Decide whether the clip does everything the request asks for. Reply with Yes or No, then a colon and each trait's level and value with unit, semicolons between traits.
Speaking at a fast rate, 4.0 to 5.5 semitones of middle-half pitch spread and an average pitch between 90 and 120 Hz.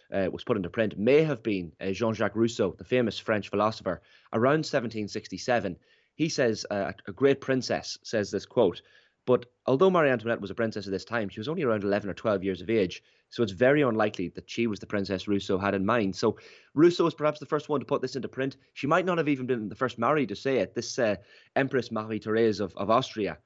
Yes: fast, 235 wpm; average, 4.7 semitones; low, 115 Hz